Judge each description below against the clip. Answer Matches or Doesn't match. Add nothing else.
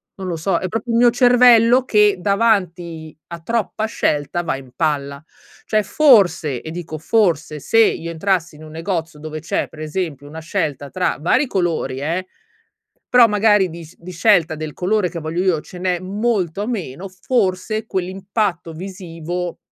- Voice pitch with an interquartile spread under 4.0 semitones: Doesn't match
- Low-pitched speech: Doesn't match